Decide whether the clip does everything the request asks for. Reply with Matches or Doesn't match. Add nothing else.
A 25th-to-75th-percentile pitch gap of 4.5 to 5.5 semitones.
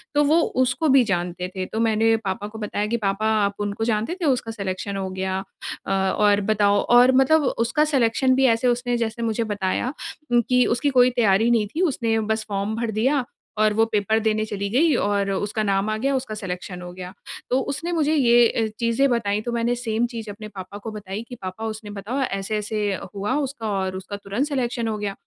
Doesn't match